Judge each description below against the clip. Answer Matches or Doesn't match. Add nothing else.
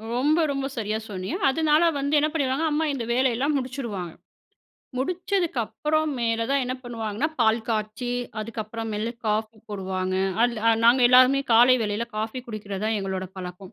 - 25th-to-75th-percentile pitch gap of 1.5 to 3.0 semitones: Doesn't match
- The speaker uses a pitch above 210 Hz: Matches